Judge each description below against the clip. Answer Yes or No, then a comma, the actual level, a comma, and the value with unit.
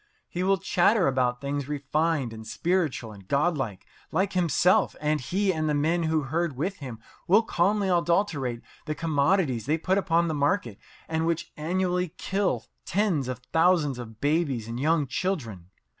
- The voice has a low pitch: No, medium, 160 Hz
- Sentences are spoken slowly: No, average, 160 wpm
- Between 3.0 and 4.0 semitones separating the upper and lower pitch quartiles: No, average, 5.0 semitones